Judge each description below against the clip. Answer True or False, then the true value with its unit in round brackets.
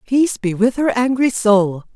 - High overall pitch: True (230 Hz)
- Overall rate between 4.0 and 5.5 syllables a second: True (4.6 syllables/s)